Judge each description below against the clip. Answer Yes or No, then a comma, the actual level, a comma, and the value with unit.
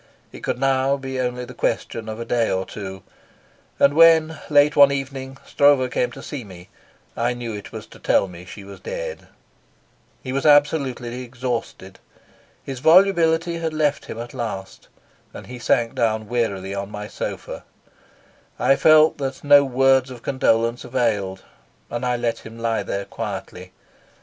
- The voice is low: Yes, low, 125 Hz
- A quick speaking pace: No, average, 165 wpm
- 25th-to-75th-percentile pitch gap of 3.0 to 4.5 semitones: Yes, average, 3.8 semitones